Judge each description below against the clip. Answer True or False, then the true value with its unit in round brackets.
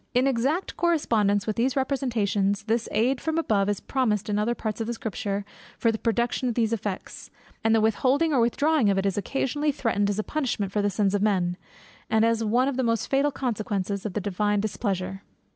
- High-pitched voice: True (220 Hz)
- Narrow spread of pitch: False (3.8 semitones)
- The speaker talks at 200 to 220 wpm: True (205 wpm)